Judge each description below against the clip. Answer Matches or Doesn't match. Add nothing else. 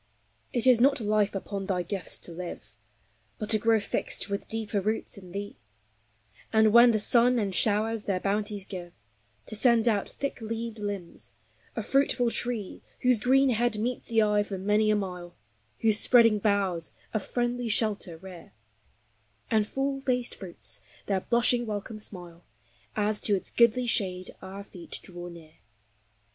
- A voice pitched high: Matches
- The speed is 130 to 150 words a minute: Doesn't match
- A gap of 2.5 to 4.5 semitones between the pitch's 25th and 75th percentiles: Matches